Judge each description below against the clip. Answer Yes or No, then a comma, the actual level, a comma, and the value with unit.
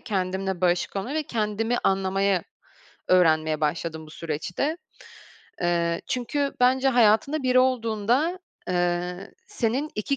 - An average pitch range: No, wide, 6.2 semitones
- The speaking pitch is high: Yes, high, 200 Hz